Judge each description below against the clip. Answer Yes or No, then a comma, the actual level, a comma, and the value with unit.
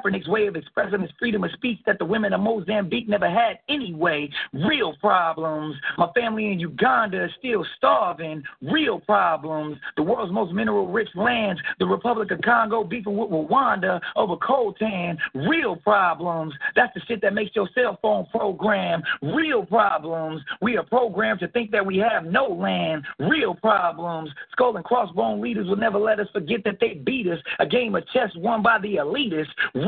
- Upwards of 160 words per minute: Yes, average, 175 wpm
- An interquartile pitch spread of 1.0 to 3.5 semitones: No, average, 4.6 semitones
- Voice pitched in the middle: No, high, 205 Hz